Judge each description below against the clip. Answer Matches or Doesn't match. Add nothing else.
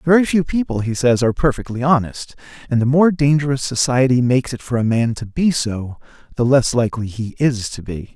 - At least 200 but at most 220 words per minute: Matches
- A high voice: Doesn't match